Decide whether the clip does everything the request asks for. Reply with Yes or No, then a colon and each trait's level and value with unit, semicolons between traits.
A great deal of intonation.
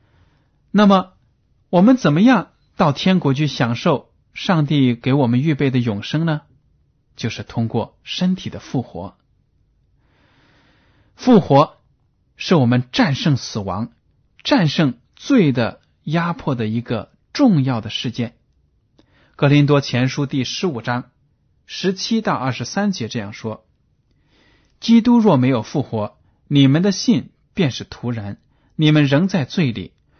Yes: wide, 6.7 semitones